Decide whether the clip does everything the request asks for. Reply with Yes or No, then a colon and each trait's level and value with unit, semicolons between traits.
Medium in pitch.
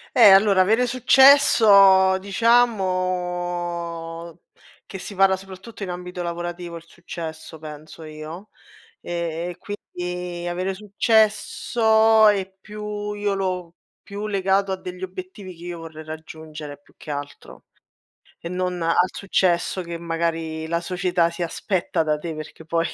Yes: medium, 180 Hz